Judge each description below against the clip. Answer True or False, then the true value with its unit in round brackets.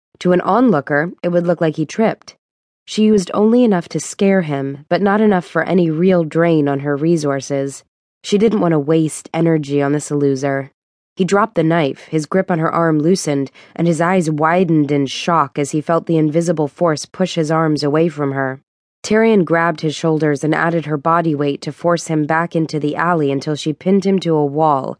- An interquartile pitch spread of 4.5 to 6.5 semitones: False (2.9 semitones)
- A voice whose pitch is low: False (160 Hz)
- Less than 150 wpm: False (205 wpm)